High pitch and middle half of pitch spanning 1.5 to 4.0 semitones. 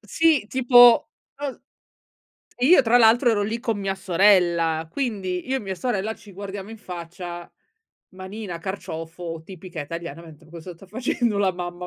No: high, 195 Hz; average, 4.6 semitones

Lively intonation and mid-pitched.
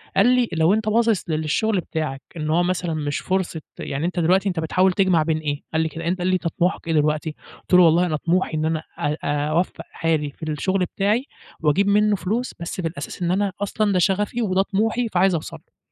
No: average, 3.7 semitones; medium, 175 Hz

